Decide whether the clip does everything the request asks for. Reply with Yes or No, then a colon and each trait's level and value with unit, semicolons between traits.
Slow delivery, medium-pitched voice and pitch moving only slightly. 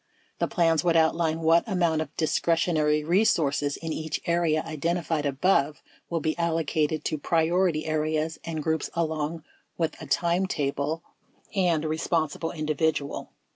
Yes: slow, 130 wpm; medium, 160 Hz; narrow, 1.6 semitones